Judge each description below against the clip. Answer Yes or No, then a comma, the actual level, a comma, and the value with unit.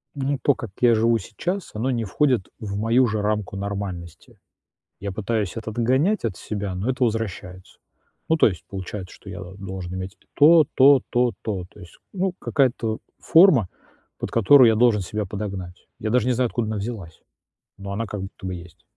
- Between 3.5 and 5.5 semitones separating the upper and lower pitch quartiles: Yes, average, 4.4 semitones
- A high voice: No, low, 110 Hz